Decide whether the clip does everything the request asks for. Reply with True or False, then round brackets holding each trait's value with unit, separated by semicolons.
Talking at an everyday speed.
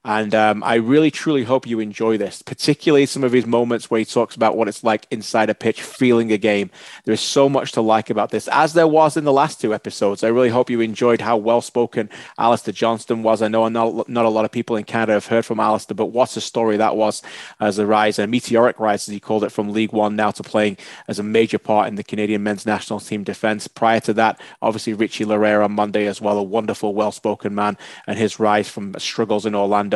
False (245 wpm)